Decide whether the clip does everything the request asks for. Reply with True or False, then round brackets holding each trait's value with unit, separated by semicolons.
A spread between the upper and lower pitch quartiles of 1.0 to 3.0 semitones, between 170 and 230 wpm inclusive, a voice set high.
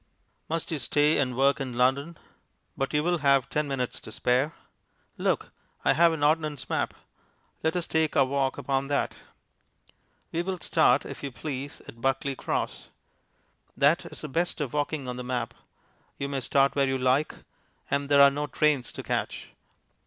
False (2.4 semitones; 175 wpm; 140 Hz)